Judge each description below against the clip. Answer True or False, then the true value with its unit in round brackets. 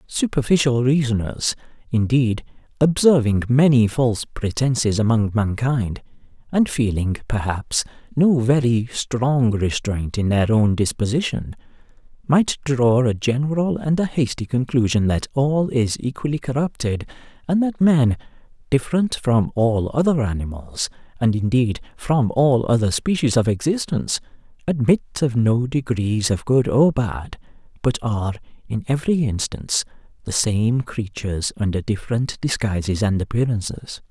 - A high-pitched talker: False (120 Hz)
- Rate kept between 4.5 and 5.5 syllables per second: True (4.6 syllables/s)